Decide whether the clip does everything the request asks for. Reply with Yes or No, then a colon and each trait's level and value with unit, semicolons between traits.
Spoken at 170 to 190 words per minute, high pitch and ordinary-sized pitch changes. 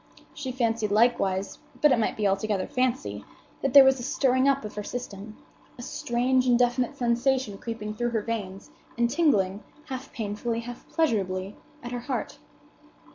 No: average, 155 wpm; high, 240 Hz; average, 3.6 semitones